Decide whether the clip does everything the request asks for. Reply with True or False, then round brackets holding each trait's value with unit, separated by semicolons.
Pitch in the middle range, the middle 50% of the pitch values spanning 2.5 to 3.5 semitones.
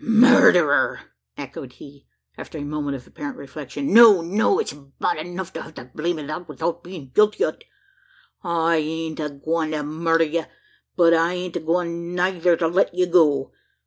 True (165 Hz; 2.9 semitones)